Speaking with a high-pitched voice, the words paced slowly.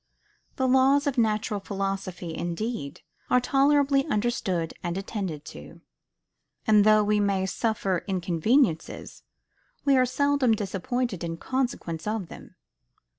Yes: high, 210 Hz; slow, 120 wpm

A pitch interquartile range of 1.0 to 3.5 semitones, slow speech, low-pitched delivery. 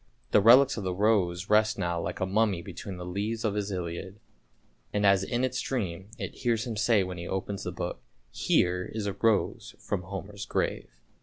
No: average, 3.0 semitones; fast, 205 wpm; low, 100 Hz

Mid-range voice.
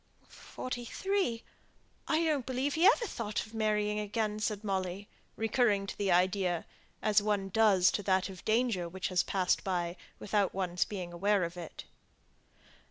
No: high, 205 Hz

